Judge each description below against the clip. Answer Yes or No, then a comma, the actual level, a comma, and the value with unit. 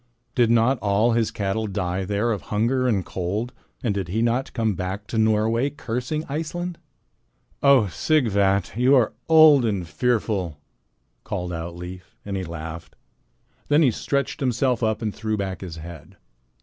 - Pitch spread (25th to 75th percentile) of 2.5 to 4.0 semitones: No, average, 4.7 semitones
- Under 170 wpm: Yes, average, 160 wpm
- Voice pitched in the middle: No, low, 110 Hz